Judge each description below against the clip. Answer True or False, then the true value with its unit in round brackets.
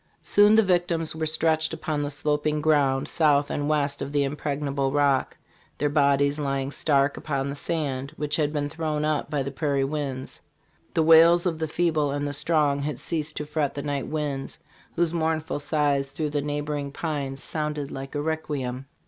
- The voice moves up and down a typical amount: False (2.0 semitones)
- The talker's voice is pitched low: False (145 Hz)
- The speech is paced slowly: False (180 wpm)